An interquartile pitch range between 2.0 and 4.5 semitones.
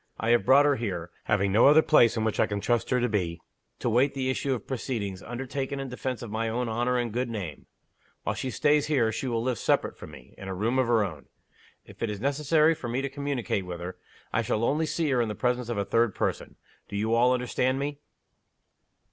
Yes: average, 3.6 semitones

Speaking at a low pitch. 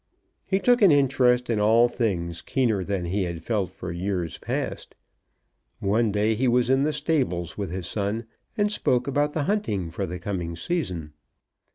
Yes: low, 110 Hz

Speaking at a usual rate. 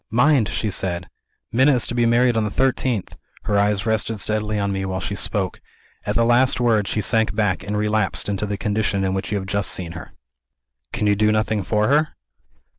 No: fast, 210 wpm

